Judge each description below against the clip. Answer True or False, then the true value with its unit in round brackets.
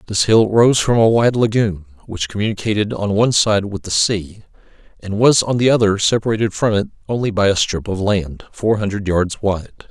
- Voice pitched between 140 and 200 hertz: False (105 Hz)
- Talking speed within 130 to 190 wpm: False (200 wpm)